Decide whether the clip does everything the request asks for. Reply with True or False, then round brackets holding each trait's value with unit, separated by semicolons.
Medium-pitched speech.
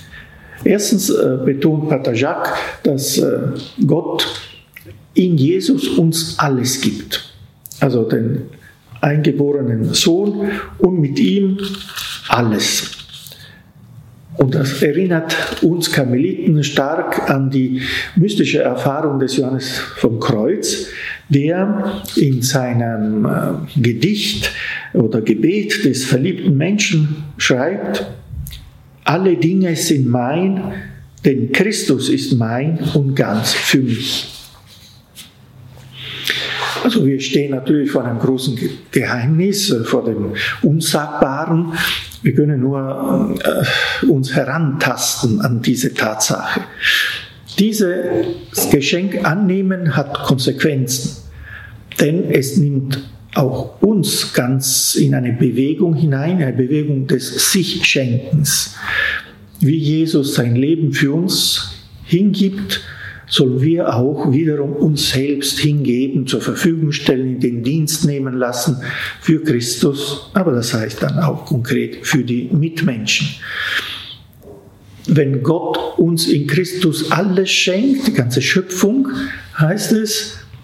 True (145 Hz)